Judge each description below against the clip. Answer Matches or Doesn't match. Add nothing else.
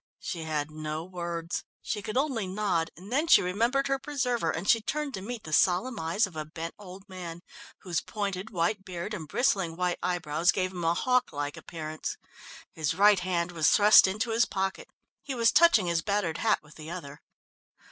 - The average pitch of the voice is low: Doesn't match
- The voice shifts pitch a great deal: Doesn't match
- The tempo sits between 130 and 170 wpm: Doesn't match